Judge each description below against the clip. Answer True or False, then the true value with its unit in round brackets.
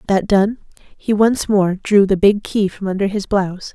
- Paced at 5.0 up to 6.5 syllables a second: False (4.6 syllables/s)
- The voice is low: False (200 Hz)